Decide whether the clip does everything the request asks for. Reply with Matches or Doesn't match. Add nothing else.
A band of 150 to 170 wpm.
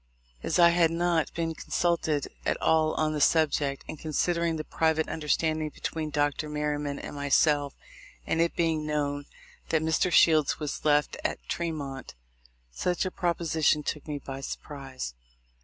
Matches